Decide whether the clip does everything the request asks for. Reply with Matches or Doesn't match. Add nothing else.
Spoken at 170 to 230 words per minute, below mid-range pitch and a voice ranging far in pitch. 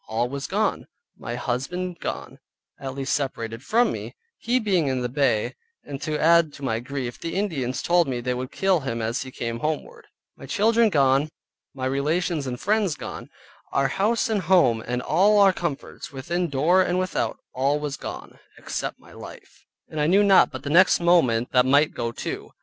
Doesn't match